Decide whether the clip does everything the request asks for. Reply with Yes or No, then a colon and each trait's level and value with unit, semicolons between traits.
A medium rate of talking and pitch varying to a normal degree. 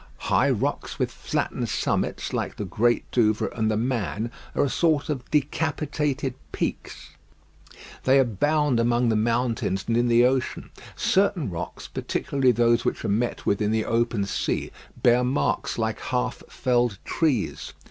Yes: average, 150 wpm; average, 3.3 semitones